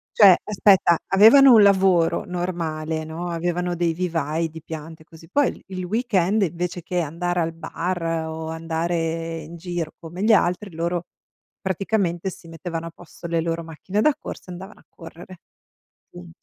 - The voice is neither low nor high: Yes, medium, 170 Hz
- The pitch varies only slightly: Yes, narrow, 2.1 semitones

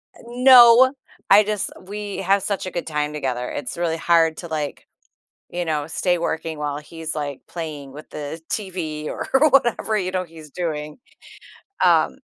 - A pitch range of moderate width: Yes, average, 4.3 semitones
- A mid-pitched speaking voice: Yes, medium, 165 Hz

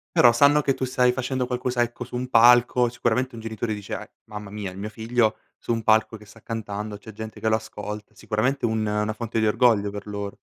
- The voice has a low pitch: Yes, low, 110 Hz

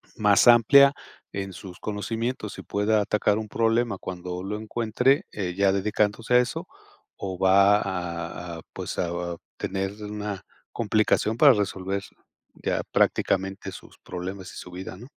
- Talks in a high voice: No, low, 100 Hz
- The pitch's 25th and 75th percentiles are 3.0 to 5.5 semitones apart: No, narrow, 2.6 semitones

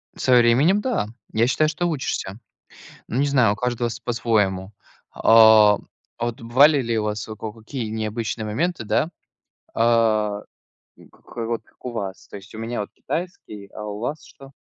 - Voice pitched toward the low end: Yes, low, 115 Hz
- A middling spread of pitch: Yes, average, 3.2 semitones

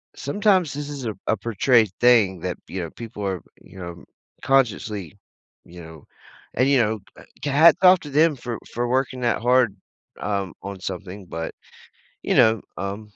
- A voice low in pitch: Yes, low, 110 Hz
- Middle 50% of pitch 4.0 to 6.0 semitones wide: Yes, average, 5.3 semitones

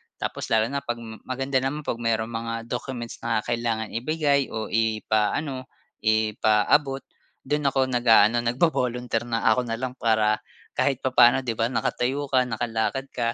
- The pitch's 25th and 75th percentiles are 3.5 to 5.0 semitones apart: No, average, 2.8 semitones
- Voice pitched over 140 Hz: No, low, 120 Hz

